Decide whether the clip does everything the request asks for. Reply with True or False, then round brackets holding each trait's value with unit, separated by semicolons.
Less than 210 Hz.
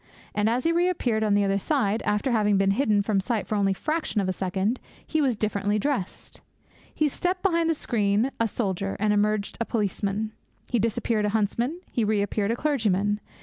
False (215 Hz)